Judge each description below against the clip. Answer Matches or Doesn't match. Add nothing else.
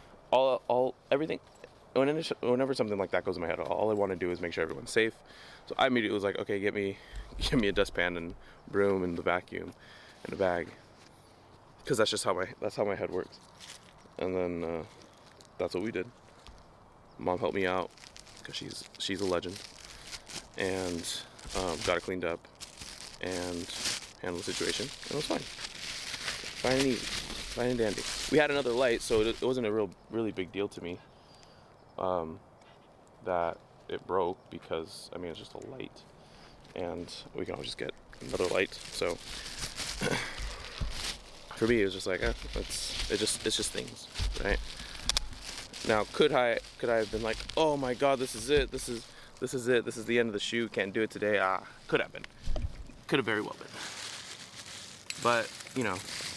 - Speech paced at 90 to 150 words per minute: Doesn't match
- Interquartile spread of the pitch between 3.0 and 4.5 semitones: Doesn't match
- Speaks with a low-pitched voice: Matches